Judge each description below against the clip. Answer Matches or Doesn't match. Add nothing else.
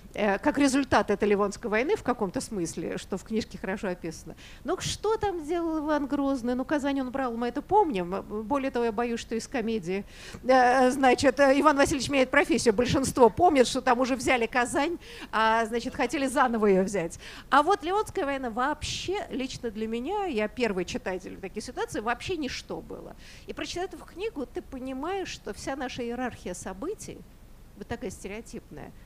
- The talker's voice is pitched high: Matches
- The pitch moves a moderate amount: Matches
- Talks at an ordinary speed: Doesn't match